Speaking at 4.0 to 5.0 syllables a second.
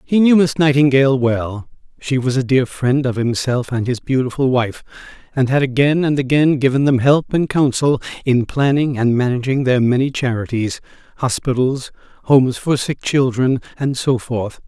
Yes: 4.9 syllables/s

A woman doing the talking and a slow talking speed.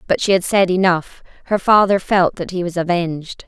No: female; fast, 205 wpm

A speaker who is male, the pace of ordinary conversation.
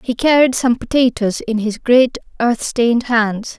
No: female; average, 165 wpm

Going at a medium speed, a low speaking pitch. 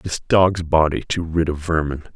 Yes: average, 165 wpm; very low, 80 Hz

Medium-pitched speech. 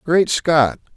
Yes: medium, 150 Hz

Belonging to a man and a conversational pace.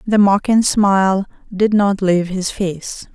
No: female; average, 155 wpm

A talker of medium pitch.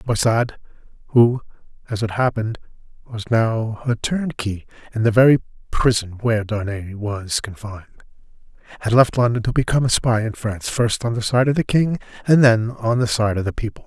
No: low, 115 Hz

